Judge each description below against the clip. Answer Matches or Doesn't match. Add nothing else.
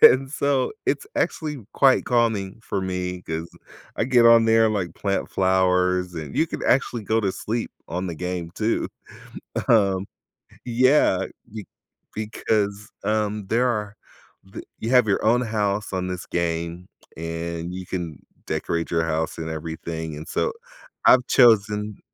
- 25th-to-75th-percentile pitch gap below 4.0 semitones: Doesn't match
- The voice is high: Doesn't match